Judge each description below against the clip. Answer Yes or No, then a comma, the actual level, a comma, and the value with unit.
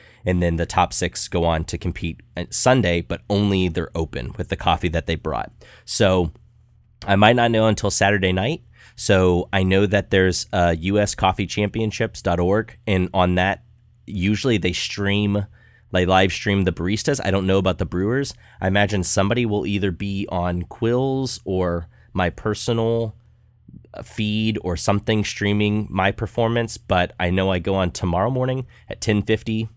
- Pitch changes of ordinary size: Yes, average, 3.5 semitones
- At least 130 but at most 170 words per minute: Yes, average, 160 wpm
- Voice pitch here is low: Yes, low, 100 Hz